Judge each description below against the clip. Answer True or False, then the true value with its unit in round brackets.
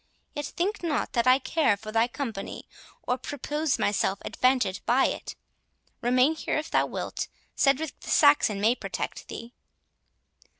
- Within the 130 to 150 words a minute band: True (140 wpm)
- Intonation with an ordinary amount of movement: True (4.2 semitones)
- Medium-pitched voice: False (255 Hz)